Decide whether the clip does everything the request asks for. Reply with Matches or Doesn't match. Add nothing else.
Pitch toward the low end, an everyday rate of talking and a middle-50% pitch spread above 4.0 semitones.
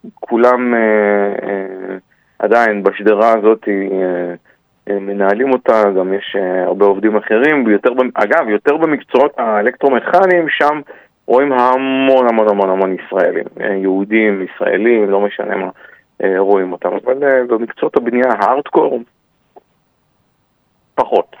Matches